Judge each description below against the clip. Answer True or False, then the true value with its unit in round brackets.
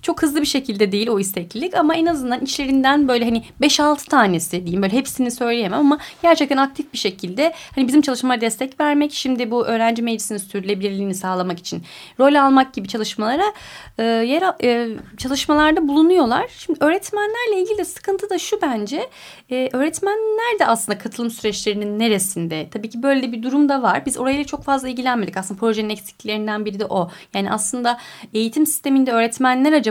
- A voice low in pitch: False (255 Hz)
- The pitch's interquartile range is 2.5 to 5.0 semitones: False (5.5 semitones)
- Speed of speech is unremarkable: False (170 wpm)